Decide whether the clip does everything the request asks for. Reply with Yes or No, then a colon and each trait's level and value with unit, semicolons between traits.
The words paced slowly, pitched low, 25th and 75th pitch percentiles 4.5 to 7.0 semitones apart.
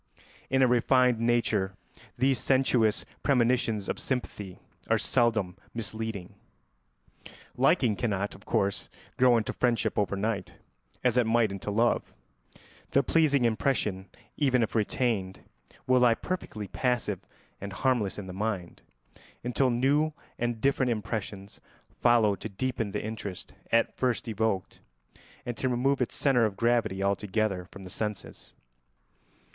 No: slow, 130 wpm; low, 115 Hz; average, 3.7 semitones